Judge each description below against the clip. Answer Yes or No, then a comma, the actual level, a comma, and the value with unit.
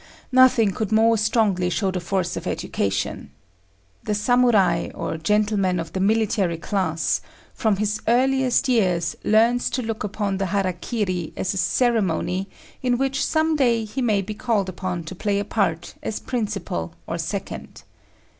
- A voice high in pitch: Yes, high, 205 Hz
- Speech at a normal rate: Yes, average, 155 wpm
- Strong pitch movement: No, average, 3.8 semitones